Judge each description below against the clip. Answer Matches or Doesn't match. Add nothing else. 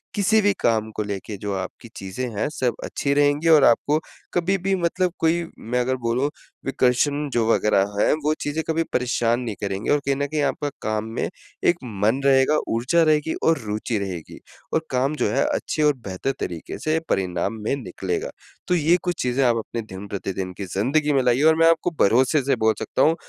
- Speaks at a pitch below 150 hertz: Matches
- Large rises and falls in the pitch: Matches